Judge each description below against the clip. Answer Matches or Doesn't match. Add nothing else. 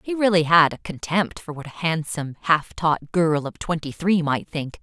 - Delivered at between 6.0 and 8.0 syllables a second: Doesn't match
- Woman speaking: Matches